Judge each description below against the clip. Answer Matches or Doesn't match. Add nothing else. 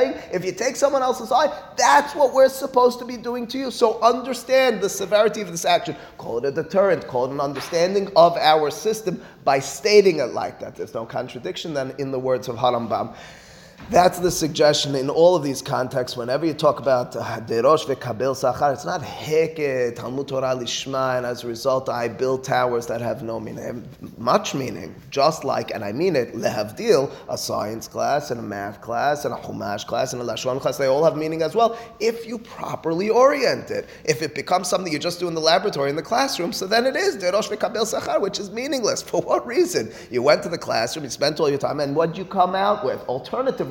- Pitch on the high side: Doesn't match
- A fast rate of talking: Matches